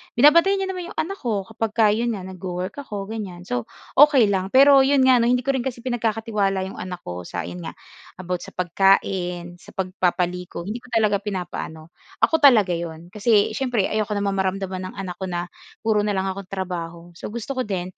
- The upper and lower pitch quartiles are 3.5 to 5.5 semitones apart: Yes, average, 4.7 semitones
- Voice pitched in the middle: No, high, 195 Hz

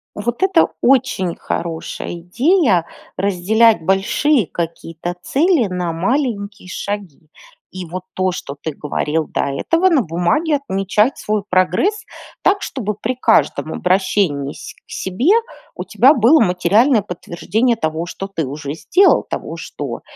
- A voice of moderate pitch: No, high, 195 Hz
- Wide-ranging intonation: Yes, wide, 6.4 semitones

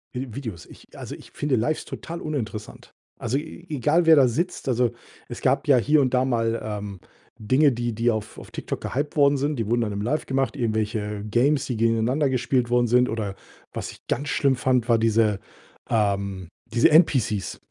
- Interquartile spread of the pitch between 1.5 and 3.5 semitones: No, average, 4.0 semitones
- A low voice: Yes, low, 120 Hz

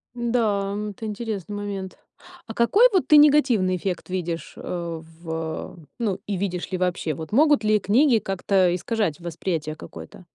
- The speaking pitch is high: Yes, high, 195 Hz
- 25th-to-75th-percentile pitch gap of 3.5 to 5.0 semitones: Yes, average, 4.4 semitones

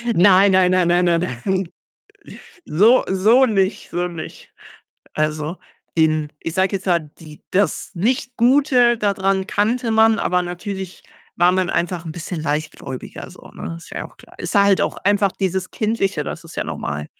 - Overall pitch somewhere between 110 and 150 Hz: No, medium, 185 Hz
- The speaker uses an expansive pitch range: No, average, 3.3 semitones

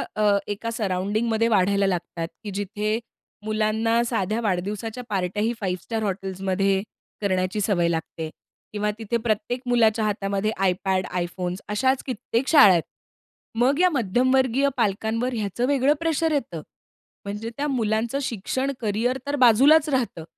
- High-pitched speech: Yes, high, 215 Hz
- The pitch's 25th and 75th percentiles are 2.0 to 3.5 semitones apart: No, average, 3.9 semitones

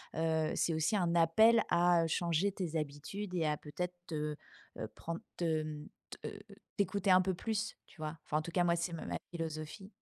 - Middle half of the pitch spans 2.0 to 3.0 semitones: Yes, average, 2.7 semitones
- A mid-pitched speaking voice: Yes, medium, 170 Hz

